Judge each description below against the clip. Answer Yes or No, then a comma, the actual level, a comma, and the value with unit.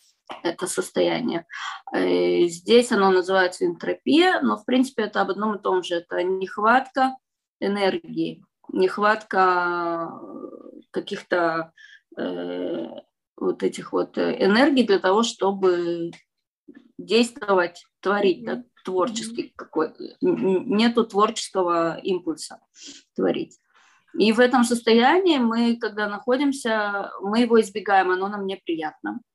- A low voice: No, high, 200 Hz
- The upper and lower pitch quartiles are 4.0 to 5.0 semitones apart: Yes, average, 4.6 semitones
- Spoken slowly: Yes, slow, 100 wpm